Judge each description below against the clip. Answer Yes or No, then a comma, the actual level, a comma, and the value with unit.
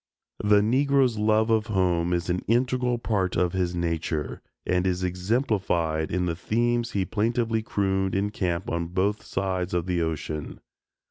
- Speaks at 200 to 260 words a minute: No, average, 155 wpm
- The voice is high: No, very low, 95 Hz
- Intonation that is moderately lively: Yes, average, 4.1 semitones